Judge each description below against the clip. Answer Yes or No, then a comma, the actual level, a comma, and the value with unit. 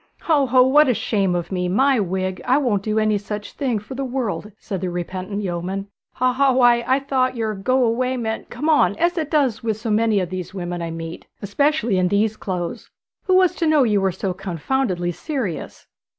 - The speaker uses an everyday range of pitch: No, wide, 5.7 semitones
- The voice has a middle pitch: No, high, 220 Hz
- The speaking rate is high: Yes, fast, 210 wpm